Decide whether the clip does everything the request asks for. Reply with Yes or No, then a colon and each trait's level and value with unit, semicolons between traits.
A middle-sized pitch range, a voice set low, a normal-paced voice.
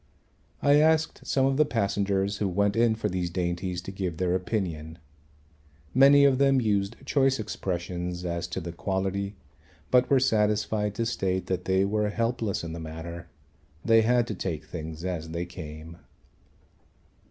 Yes: average, 4.7 semitones; very low, 95 Hz; average, 160 wpm